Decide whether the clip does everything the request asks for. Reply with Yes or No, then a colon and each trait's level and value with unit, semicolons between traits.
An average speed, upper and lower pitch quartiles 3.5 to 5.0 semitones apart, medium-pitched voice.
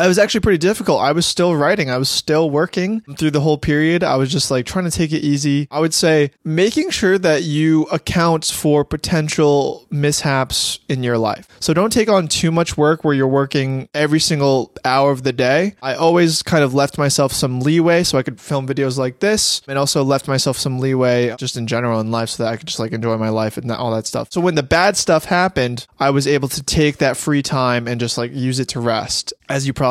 No: fast, 240 wpm; average, 3.8 semitones; medium, 145 Hz